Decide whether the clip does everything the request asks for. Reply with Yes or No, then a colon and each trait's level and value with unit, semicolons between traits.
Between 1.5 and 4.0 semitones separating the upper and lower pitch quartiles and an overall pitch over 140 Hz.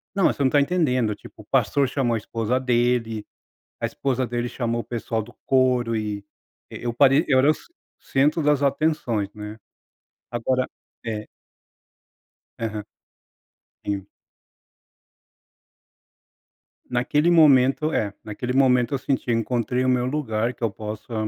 No: average, 3.2 semitones; low, 125 Hz